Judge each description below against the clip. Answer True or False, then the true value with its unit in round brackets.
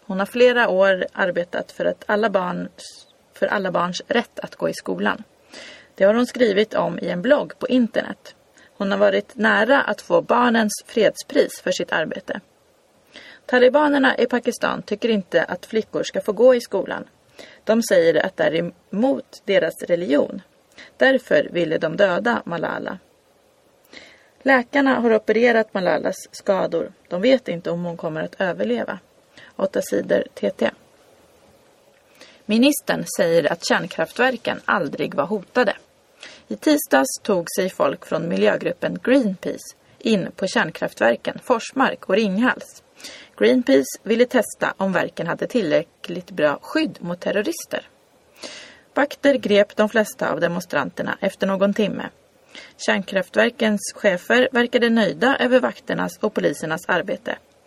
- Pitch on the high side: True (225 Hz)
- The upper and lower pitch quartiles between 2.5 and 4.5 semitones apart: False (5.1 semitones)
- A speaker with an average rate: True (135 wpm)